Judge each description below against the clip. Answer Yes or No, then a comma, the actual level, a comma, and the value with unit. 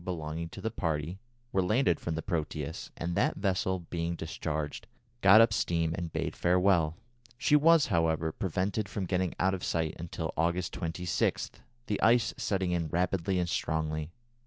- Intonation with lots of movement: No, average, 2.8 semitones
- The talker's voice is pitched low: Yes, very low, 85 Hz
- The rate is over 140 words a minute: Yes, average, 160 wpm